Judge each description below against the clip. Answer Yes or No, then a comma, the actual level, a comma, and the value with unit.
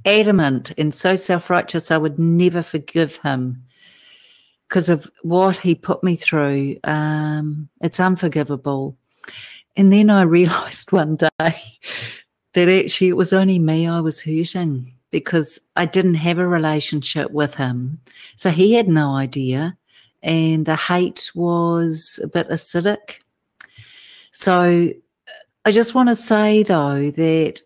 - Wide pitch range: No, average, 3.3 semitones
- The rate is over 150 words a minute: No, slow, 135 wpm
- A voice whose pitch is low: No, medium, 170 Hz